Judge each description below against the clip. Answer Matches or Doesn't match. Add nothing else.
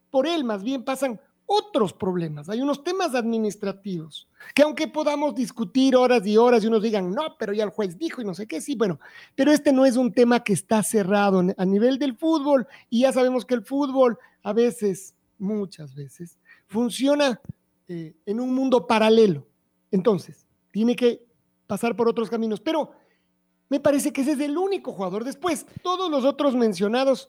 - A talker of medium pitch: Doesn't match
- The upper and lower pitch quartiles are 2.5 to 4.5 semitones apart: Doesn't match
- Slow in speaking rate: Doesn't match